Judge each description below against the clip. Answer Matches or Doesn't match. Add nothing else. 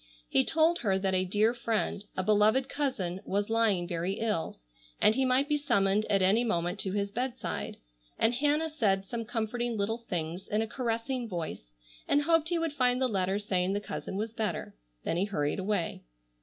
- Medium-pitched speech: Doesn't match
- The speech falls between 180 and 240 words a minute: Matches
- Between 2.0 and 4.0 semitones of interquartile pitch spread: Doesn't match